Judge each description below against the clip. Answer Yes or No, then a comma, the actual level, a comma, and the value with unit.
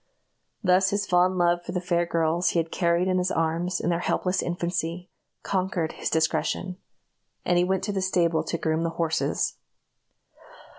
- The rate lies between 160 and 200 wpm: Yes, average, 175 wpm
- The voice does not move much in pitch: Yes, narrow, 1.6 semitones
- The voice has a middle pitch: Yes, medium, 175 Hz